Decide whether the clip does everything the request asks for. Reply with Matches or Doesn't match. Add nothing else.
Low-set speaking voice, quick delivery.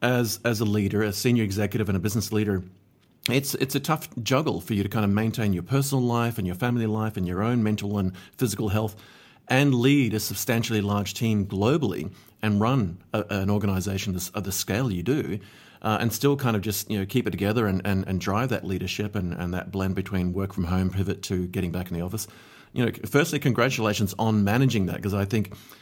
Matches